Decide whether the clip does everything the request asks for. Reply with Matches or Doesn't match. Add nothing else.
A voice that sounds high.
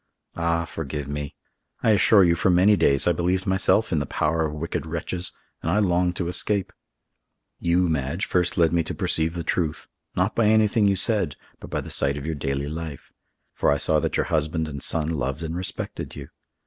Doesn't match